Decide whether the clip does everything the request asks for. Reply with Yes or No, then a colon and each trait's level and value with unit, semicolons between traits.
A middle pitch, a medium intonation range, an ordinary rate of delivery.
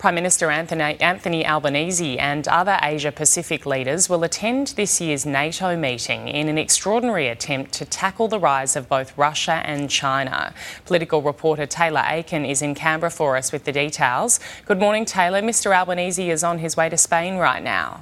Yes: medium, 160 Hz; average, 3.5 semitones; average, 175 wpm